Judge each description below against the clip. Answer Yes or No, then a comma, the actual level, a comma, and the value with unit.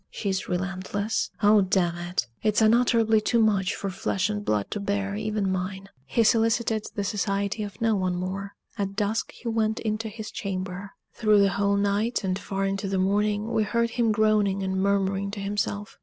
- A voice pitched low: No, high, 200 Hz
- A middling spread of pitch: No, narrow, 1.9 semitones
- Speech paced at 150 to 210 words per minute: Yes, average, 185 wpm